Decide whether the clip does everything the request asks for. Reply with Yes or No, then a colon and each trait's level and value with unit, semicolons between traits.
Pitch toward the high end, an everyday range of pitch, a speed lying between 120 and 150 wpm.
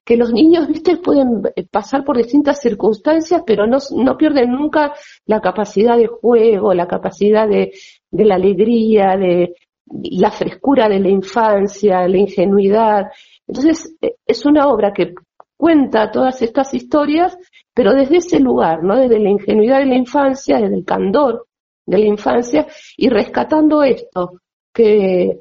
No: high, 235 Hz; wide, 6.2 semitones; average, 145 wpm